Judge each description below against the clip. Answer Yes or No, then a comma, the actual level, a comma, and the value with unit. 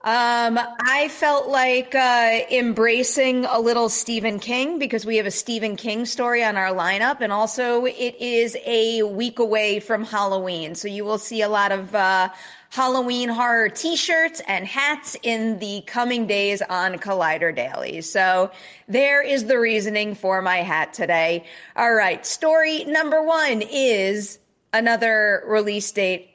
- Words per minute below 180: Yes, average, 155 wpm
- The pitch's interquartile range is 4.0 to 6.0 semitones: No, average, 3.6 semitones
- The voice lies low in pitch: No, high, 225 Hz